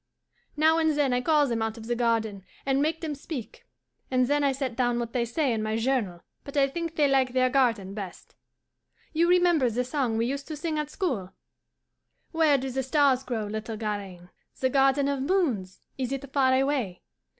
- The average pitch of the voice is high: Yes, very high, 260 Hz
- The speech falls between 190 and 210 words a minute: Yes, average, 200 wpm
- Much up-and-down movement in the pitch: No, average, 4.1 semitones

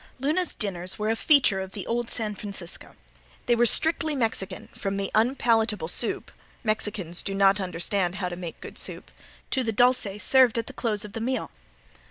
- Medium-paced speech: Yes, average, 185 wpm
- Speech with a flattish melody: No, average, 3.7 semitones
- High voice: Yes, high, 215 Hz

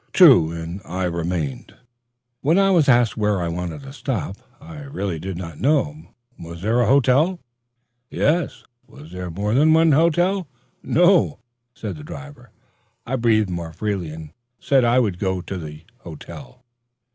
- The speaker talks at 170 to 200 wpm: No, average, 150 wpm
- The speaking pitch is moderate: No, low, 105 Hz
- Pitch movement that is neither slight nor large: No, wide, 8.7 semitones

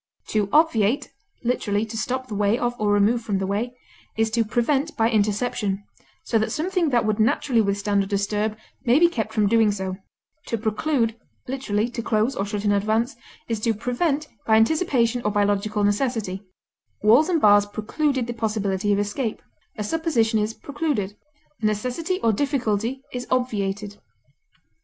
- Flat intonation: No, average, 3.3 semitones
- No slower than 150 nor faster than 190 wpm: Yes, average, 165 wpm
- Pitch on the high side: Yes, high, 220 Hz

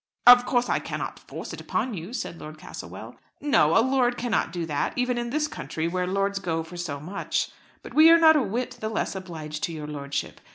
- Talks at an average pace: No, fast, 220 wpm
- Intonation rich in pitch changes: Yes, wide, 7.3 semitones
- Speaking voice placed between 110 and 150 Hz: No, high, 195 Hz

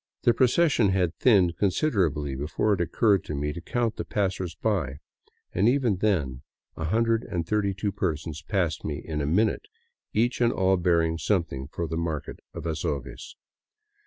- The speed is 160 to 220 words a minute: No, average, 145 wpm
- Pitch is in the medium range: No, very low, 90 Hz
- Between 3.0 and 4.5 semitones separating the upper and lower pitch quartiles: No, average, 5.1 semitones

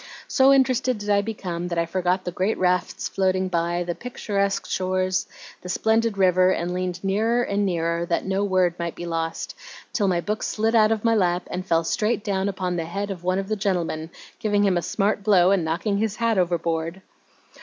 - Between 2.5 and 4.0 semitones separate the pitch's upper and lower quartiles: Yes, average, 3.0 semitones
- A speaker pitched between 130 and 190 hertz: Yes, medium, 185 Hz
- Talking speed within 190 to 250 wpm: Yes, fast, 205 wpm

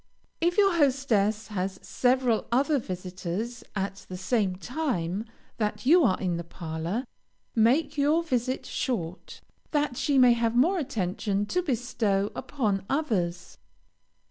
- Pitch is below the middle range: No, high, 230 Hz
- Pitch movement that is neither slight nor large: No, wide, 6.2 semitones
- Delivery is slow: Yes, slow, 130 wpm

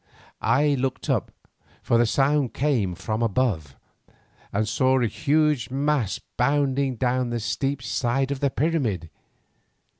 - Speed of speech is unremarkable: No, slow, 130 wpm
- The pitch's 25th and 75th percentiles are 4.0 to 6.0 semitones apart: No, average, 3.4 semitones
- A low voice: Yes, low, 130 Hz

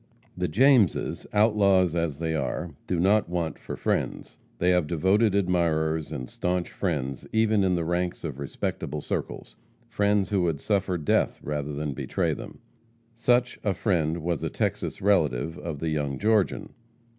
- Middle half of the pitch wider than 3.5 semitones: Yes, average, 4.4 semitones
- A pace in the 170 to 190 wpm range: No, average, 155 wpm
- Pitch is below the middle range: Yes, very low, 85 Hz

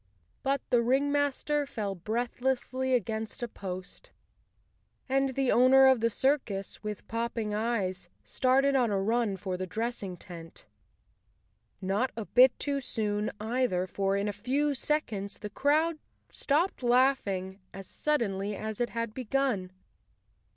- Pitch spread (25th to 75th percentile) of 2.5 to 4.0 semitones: No, average, 4.8 semitones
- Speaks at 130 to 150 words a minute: Yes, slow, 135 wpm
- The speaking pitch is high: Yes, high, 235 Hz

